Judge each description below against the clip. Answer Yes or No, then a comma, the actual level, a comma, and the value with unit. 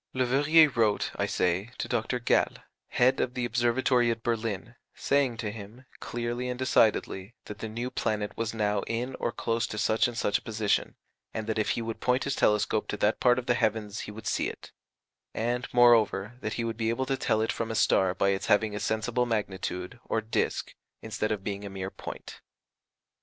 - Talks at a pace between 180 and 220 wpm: Yes, fast, 205 wpm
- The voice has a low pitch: Yes, low, 115 Hz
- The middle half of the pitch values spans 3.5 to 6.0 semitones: No, narrow, 2.5 semitones